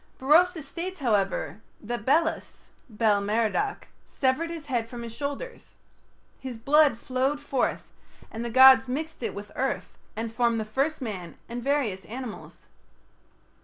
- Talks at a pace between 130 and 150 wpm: Yes, average, 140 wpm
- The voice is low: No, very high, 255 Hz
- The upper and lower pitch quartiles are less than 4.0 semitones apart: No, average, 4.5 semitones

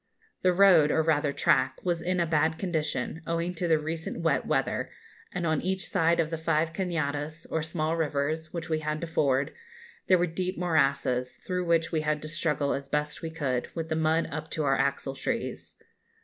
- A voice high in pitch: No, medium, 160 Hz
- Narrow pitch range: Yes, narrow, 2.1 semitones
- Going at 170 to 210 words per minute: Yes, average, 195 wpm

